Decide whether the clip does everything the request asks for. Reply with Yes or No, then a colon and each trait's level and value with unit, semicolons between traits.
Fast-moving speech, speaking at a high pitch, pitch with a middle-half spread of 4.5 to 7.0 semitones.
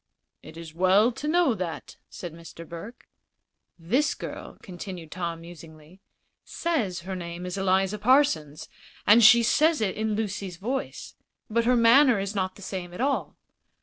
No: average, 155 wpm; high, 195 Hz; average, 5.2 semitones